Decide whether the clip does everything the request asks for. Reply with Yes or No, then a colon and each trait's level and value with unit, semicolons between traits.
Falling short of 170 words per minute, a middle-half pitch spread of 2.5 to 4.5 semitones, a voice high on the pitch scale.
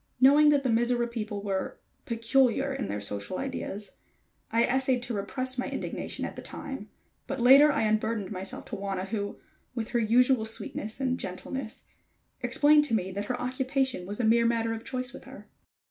No: average, 180 wpm; average, 3.8 semitones; high, 235 Hz